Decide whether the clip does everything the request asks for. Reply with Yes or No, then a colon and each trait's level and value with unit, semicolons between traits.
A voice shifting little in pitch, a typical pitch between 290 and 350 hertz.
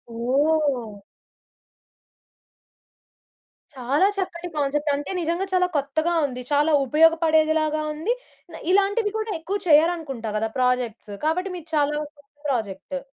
No: average, 4.0 semitones; very high, 300 Hz